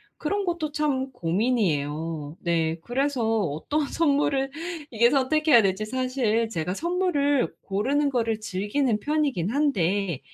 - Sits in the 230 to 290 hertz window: Yes, high, 240 Hz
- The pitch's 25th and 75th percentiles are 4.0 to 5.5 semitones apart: No, wide, 7.1 semitones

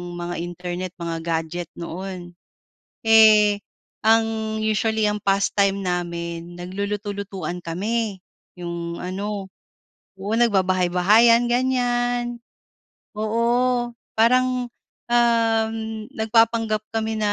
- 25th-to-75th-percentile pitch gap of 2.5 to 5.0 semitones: Yes, average, 4.1 semitones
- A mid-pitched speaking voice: No, high, 210 Hz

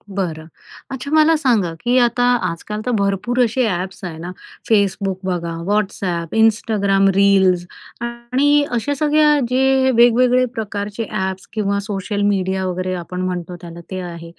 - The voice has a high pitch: Yes, high, 200 Hz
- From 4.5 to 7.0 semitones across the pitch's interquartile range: Yes, average, 4.8 semitones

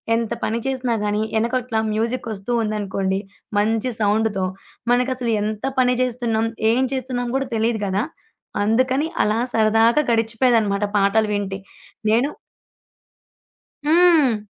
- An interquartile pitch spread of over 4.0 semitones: No, average, 2.9 semitones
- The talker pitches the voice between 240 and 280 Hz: No, high, 225 Hz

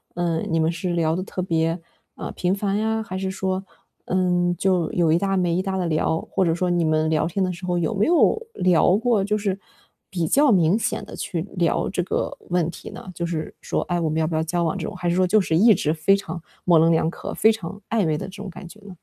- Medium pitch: Yes, medium, 180 Hz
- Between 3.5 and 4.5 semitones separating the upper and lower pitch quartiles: No, average, 2.8 semitones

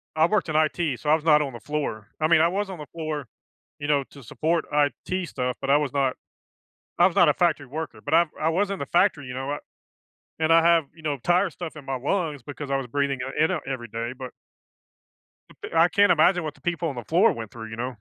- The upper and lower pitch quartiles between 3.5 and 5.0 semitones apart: Yes, average, 3.8 semitones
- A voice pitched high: No, medium, 150 Hz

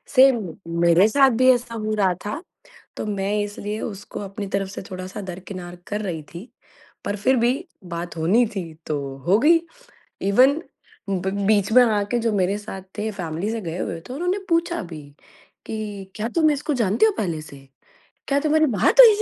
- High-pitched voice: Yes, high, 205 Hz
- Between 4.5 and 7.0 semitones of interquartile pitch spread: Yes, average, 5.1 semitones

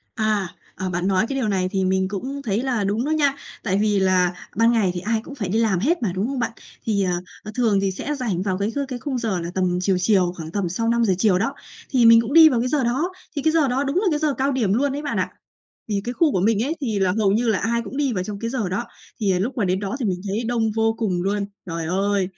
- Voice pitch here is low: No, high, 220 Hz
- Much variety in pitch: No, average, 4.8 semitones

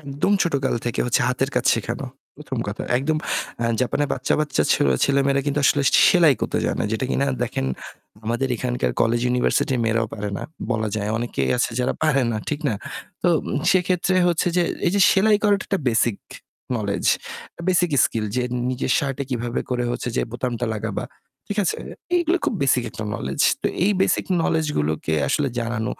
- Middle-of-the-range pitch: No, low, 130 Hz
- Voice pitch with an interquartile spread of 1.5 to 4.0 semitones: No, average, 4.8 semitones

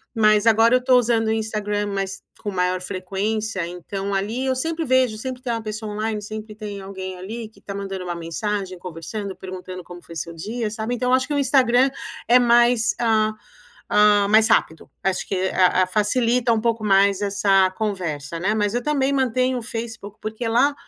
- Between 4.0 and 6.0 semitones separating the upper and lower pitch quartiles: No, average, 3.4 semitones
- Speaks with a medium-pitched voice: No, high, 215 Hz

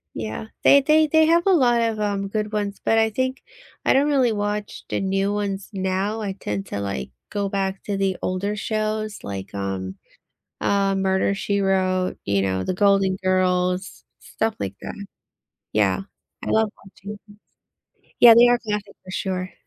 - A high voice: Yes, high, 200 Hz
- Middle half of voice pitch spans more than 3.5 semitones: No, narrow, 2.6 semitones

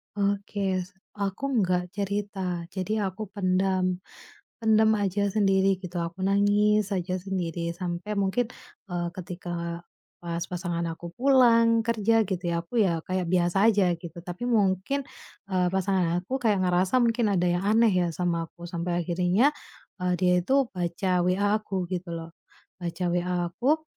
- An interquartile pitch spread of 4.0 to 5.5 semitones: No, average, 2.8 semitones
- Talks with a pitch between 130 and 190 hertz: Yes, medium, 185 Hz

